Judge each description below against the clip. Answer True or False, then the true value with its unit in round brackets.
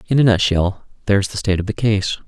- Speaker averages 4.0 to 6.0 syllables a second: False (6.5 syllables/s)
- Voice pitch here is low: True (100 Hz)